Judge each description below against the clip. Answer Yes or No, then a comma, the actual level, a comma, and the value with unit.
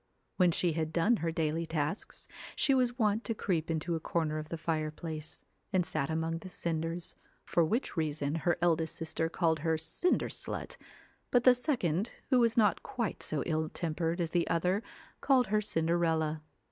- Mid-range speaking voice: Yes, medium, 165 Hz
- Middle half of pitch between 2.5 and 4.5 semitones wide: Yes, average, 3.4 semitones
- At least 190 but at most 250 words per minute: No, average, 175 wpm